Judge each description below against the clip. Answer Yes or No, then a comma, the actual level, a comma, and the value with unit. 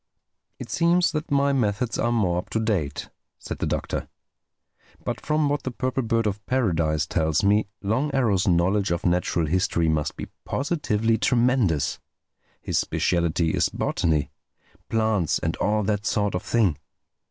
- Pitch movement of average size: No, wide, 6.3 semitones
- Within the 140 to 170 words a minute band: Yes, average, 150 wpm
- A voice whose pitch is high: No, low, 105 Hz